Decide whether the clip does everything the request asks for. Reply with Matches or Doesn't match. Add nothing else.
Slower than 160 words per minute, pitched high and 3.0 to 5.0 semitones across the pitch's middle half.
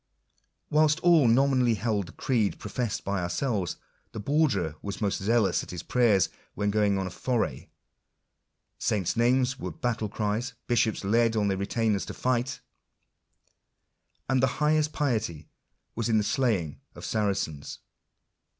Doesn't match